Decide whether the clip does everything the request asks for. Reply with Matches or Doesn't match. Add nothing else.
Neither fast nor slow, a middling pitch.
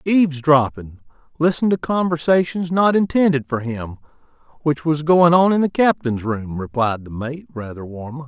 Matches